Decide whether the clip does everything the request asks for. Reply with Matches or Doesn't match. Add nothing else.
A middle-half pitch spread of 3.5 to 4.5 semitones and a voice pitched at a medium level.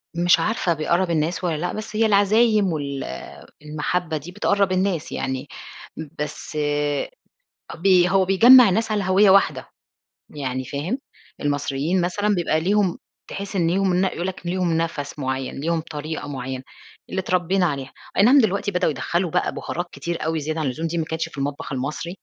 Matches